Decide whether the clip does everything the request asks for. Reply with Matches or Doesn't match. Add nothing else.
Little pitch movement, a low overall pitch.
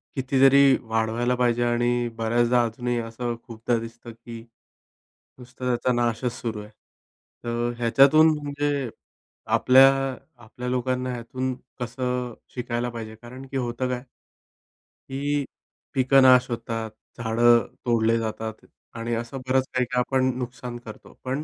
Matches